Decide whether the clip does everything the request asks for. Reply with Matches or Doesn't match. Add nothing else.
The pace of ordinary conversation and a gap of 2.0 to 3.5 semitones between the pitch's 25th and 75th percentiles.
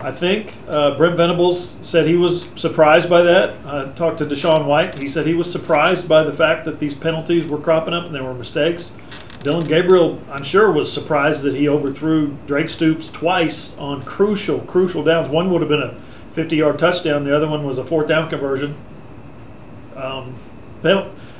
Matches